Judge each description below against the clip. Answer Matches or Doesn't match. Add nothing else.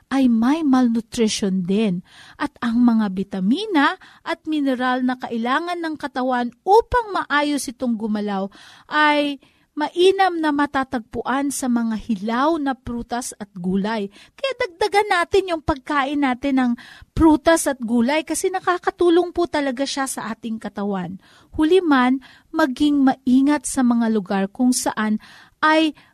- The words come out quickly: Doesn't match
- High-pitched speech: Matches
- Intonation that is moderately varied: Matches